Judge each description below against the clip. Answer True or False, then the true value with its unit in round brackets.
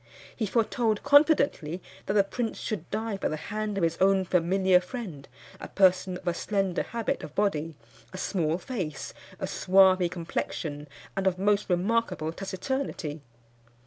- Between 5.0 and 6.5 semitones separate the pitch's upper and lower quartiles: False (3.8 semitones)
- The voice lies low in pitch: False (190 Hz)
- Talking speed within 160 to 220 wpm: False (150 wpm)